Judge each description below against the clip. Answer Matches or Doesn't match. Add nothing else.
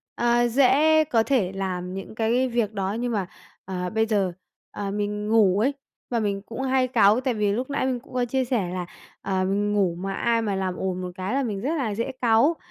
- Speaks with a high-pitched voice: Matches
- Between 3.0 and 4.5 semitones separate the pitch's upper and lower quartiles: Matches